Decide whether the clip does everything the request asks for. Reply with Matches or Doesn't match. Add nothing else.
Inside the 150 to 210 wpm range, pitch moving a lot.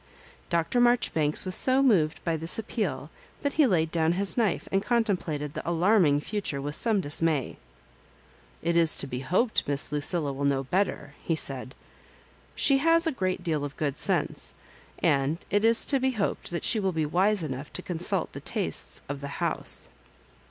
Matches